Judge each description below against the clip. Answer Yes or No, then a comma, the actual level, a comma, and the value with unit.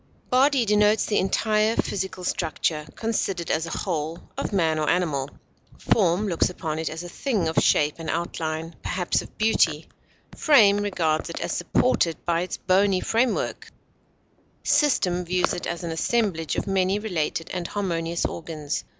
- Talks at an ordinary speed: Yes, average, 155 wpm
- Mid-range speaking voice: Yes, medium, 175 Hz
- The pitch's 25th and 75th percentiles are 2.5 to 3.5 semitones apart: No, average, 4.0 semitones